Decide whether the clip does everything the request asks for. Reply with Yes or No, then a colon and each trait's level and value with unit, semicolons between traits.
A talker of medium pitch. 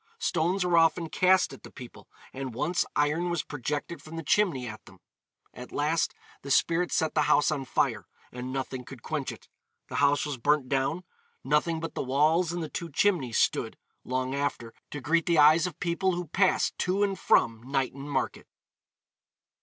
Yes: medium, 150 Hz